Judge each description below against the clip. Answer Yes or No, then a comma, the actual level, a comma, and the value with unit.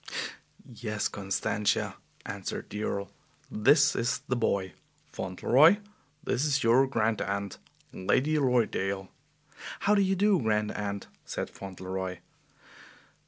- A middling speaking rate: No, slow, 115 wpm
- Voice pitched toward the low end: Yes, low, 110 Hz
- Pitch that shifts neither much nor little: No, wide, 5.7 semitones